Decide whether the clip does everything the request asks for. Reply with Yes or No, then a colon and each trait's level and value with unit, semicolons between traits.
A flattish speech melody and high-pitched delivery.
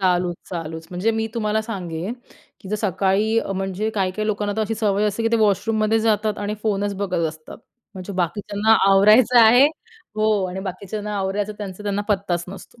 Yes: narrow, 2.3 semitones; high, 205 Hz